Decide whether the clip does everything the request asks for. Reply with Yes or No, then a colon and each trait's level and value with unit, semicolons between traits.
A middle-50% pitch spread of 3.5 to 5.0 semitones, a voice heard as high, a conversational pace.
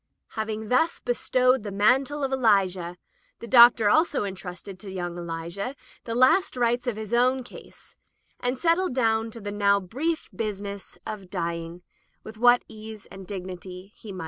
Yes: average, 4.4 semitones; high, 215 Hz; average, 170 wpm